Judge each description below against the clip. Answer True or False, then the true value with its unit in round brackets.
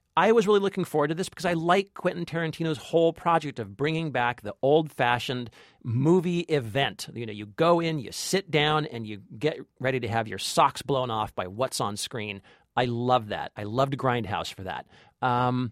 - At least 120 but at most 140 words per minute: False (200 wpm)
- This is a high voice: False (135 Hz)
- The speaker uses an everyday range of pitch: False (5.9 semitones)